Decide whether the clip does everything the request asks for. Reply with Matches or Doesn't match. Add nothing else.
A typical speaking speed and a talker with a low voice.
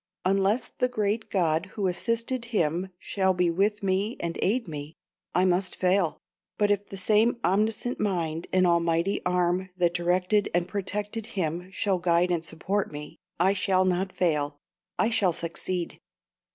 Doesn't match